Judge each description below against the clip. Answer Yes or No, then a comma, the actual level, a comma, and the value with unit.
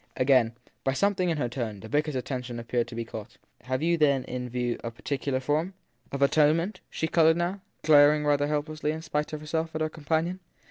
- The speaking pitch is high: No, medium, 145 Hz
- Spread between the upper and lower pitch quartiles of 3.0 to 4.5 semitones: Yes, average, 4.0 semitones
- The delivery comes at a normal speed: No, fast, 215 wpm